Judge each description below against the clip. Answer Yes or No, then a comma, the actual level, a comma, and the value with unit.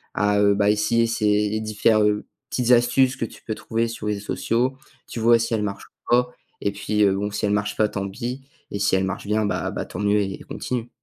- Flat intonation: Yes, narrow, 2.2 semitones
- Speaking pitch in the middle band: No, low, 105 Hz